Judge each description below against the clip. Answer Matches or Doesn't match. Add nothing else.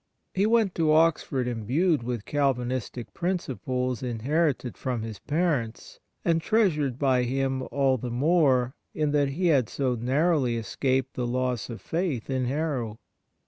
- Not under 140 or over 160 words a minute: Matches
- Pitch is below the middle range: Matches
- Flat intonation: Doesn't match